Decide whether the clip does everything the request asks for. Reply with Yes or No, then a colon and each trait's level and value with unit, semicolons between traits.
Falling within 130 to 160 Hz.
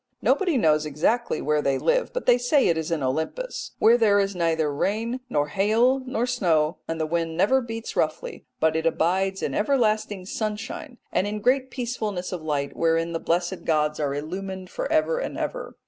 No: high, 190 Hz